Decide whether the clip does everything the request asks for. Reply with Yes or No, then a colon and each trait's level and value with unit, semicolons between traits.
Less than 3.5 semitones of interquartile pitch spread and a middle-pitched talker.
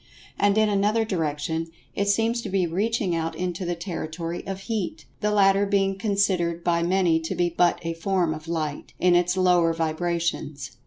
Yes: average, 3.0 semitones; medium, 175 Hz